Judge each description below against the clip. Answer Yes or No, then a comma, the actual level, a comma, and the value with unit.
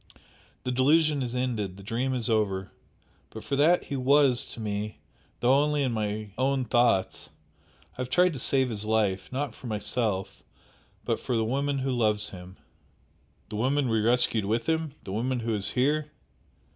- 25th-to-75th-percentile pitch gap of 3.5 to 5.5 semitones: Yes, average, 4.1 semitones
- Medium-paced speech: Yes, average, 175 wpm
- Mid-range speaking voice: No, low, 120 Hz